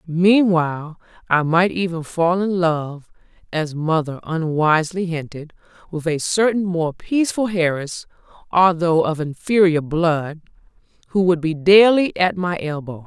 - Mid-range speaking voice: Yes, medium, 170 Hz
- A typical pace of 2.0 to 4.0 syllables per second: Yes, 3.7 syllables/s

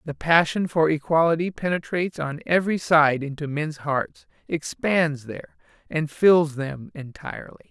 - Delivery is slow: Yes, slow, 130 wpm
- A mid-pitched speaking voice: Yes, medium, 155 Hz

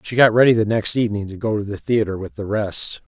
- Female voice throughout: No, male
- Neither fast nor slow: No, fast, 265 wpm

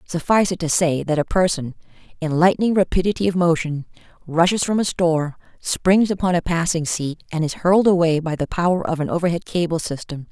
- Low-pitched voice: No, medium, 170 Hz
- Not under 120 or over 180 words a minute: No, average, 190 wpm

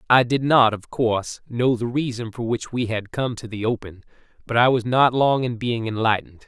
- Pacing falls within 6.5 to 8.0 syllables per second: No, 5.2 syllables/s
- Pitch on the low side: Yes, low, 120 Hz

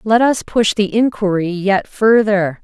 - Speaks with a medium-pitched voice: No, high, 210 Hz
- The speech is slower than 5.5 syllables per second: Yes, 4.0 syllables/s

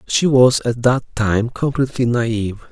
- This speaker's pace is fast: No, average, 155 wpm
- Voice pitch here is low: Yes, low, 120 Hz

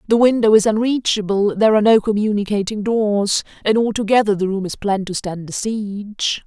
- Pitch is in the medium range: No, high, 210 Hz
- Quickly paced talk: No, average, 175 wpm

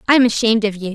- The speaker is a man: No, female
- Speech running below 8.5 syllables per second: No, 8.9 syllables/s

